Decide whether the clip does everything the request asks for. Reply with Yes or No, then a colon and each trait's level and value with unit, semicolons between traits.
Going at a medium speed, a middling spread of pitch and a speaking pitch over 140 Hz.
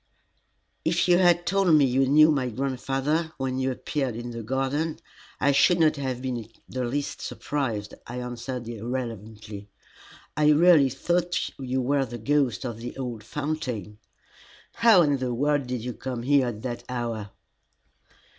No: average, 165 wpm; average, 3.6 semitones; low, 130 Hz